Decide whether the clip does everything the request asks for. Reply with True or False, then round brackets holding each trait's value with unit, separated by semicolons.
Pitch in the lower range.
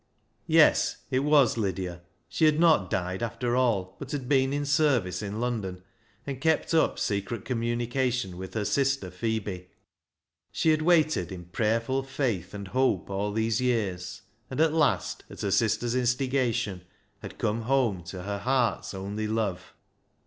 True (115 Hz)